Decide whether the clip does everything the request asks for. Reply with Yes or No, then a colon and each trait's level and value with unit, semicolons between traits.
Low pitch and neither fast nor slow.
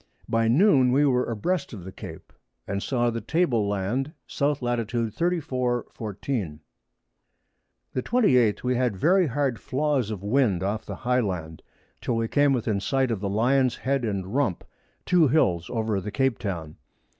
Yes: low, 120 Hz; average, 165 wpm